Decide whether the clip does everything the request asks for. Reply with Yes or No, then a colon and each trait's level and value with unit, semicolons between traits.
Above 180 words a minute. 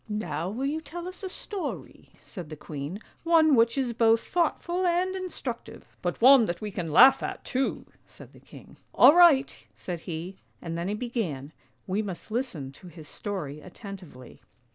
Yes: average, 190 wpm